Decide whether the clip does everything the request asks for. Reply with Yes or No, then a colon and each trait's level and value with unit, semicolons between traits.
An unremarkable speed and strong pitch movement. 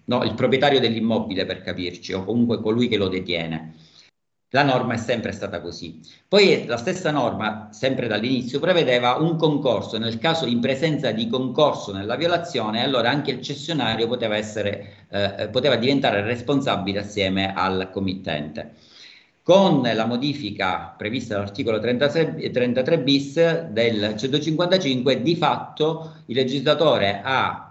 Yes: average, 135 wpm; wide, 6.0 semitones